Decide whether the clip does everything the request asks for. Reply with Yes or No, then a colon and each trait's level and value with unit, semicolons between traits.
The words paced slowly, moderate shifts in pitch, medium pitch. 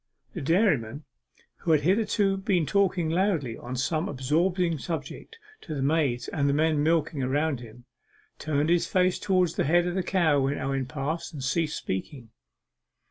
No: average, 160 wpm; average, 4.5 semitones; medium, 155 Hz